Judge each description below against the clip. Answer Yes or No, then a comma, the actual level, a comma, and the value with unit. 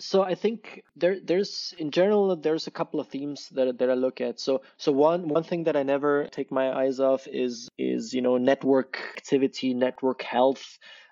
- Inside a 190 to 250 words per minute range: Yes, average, 200 wpm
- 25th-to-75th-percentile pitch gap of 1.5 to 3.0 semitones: No, average, 4.5 semitones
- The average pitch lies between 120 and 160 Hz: Yes, medium, 140 Hz